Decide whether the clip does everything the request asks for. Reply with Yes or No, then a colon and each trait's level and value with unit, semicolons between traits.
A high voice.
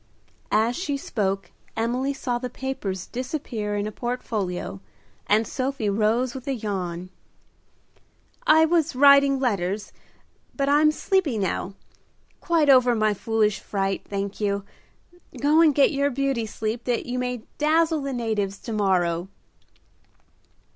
Yes: high, 240 Hz